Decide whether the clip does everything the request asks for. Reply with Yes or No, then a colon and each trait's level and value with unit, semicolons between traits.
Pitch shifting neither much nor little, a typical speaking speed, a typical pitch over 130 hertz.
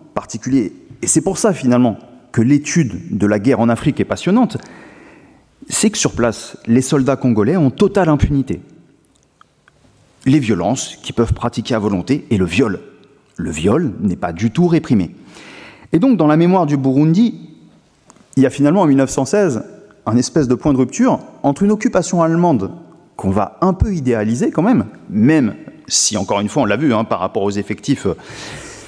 No: wide, 6.5 semitones; average, 180 wpm; medium, 140 Hz